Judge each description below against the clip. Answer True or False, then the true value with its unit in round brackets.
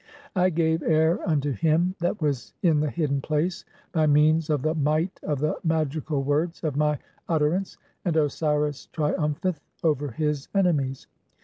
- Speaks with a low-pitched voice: False (155 Hz)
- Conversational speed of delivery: True (150 wpm)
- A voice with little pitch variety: True (1.9 semitones)